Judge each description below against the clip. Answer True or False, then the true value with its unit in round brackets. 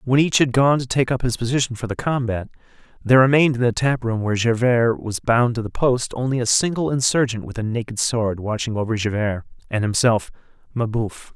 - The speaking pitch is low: True (120 Hz)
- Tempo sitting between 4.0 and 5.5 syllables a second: False (5.8 syllables/s)